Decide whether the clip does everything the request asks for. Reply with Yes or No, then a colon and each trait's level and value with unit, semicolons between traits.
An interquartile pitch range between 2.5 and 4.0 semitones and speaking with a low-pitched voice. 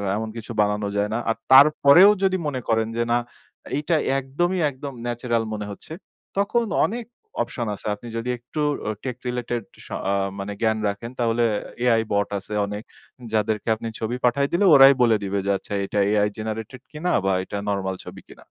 No: average, 4.5 semitones; low, 115 Hz